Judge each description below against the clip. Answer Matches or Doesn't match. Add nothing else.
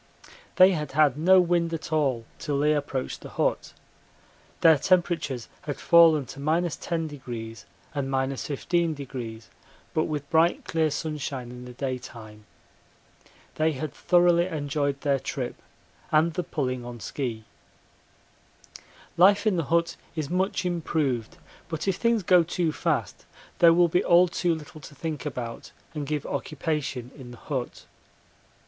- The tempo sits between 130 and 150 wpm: Matches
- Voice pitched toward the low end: Doesn't match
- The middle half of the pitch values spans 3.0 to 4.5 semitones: Matches